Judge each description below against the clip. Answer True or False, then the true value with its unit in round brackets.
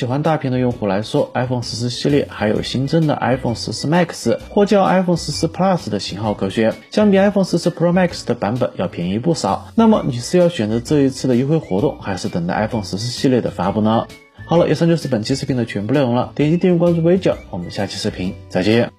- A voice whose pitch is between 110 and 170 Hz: True (135 Hz)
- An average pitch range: False (7.4 semitones)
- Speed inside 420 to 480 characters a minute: True (450 characters per minute)